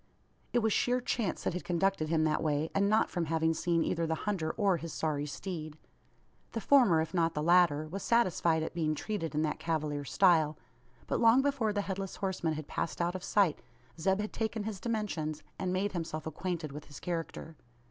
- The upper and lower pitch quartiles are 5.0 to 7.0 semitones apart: No, average, 4.1 semitones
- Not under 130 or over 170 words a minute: No, average, 200 wpm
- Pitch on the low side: No, medium, 170 Hz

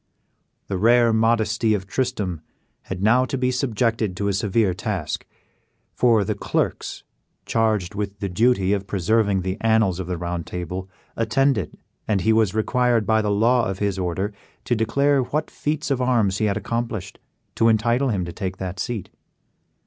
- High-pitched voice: No, low, 110 Hz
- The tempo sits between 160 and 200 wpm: Yes, average, 170 wpm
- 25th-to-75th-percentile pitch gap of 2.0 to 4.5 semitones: Yes, average, 3.6 semitones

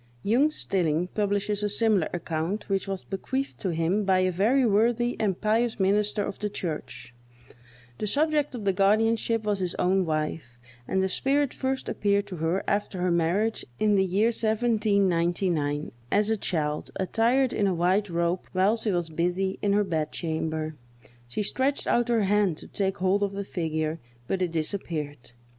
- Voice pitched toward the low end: No, high, 195 Hz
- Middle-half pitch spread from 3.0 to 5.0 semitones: Yes, average, 3.9 semitones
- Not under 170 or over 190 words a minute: Yes, average, 175 wpm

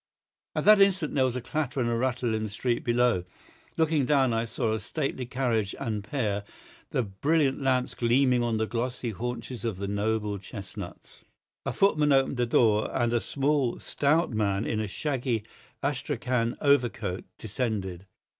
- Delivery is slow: No, average, 165 wpm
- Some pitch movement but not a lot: Yes, average, 3.6 semitones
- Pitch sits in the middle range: No, low, 120 Hz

